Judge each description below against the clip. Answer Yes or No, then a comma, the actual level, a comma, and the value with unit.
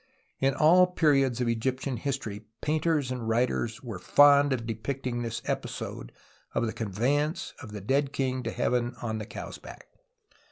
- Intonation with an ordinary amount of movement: Yes, average, 3.7 semitones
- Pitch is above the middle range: No, low, 125 Hz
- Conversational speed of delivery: Yes, average, 160 wpm